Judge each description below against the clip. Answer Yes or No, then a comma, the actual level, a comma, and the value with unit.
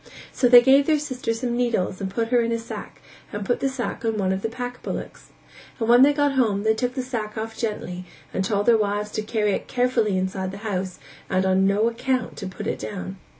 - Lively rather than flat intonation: No, average, 3.8 semitones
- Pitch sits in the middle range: No, high, 225 Hz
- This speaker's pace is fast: Yes, fast, 235 wpm